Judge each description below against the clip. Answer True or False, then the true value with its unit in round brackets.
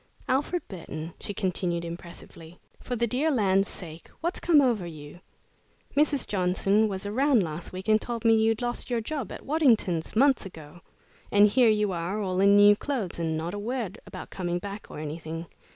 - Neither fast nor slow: True (185 wpm)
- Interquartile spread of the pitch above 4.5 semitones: True (5.4 semitones)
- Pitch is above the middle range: True (205 Hz)